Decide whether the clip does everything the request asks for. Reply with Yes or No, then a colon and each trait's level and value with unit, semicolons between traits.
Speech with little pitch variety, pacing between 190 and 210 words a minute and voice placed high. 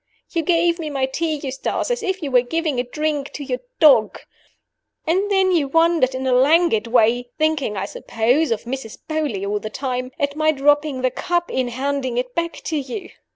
No: average, 4.4 semitones; average, 200 wpm; very high, 280 Hz